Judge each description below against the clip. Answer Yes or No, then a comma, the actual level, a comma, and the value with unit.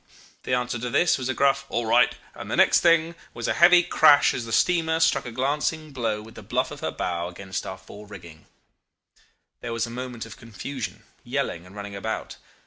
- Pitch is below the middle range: Yes, low, 120 Hz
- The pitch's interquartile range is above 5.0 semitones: Yes, wide, 5.4 semitones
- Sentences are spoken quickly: Yes, fast, 210 wpm